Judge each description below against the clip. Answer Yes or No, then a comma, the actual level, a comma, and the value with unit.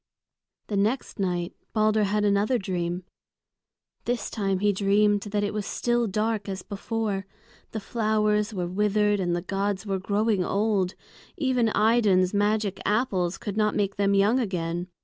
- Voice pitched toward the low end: No, high, 205 Hz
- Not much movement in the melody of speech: Yes, narrow, 1.9 semitones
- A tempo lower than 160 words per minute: Yes, average, 150 wpm